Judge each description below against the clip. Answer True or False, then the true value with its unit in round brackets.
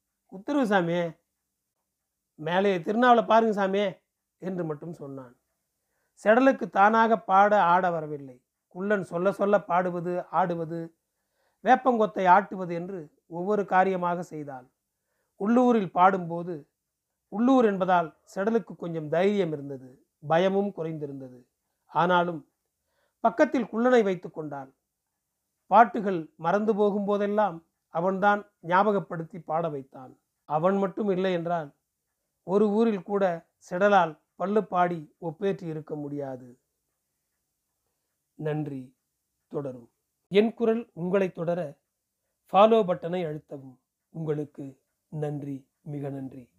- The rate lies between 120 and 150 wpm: False (95 wpm)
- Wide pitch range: False (4.8 semitones)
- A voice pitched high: False (180 Hz)